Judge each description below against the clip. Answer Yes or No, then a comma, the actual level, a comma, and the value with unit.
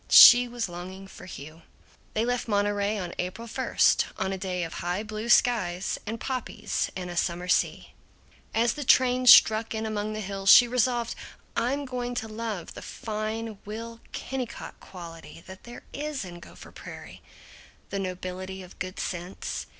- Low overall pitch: No, high, 215 Hz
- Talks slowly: No, average, 165 wpm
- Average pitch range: Yes, average, 4.2 semitones